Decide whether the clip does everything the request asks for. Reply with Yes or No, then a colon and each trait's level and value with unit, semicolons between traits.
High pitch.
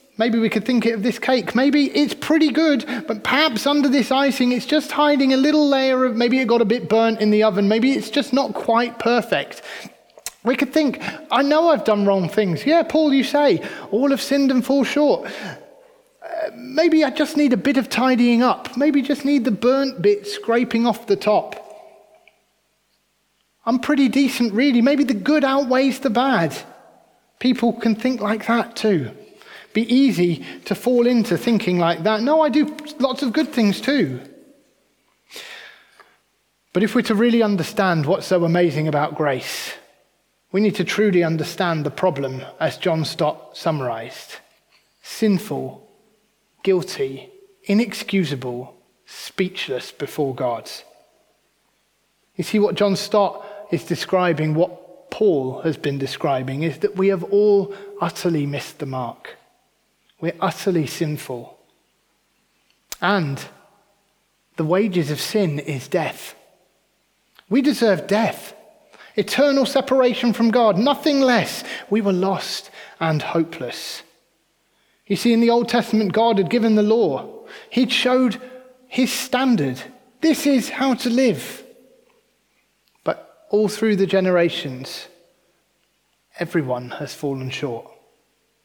Yes: high, 230 Hz